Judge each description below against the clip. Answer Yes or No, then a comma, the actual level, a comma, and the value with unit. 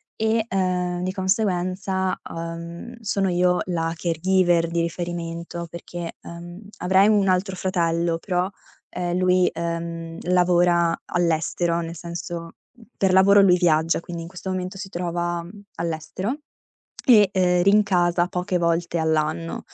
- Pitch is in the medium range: Yes, medium, 175 Hz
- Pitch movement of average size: No, narrow, 1.8 semitones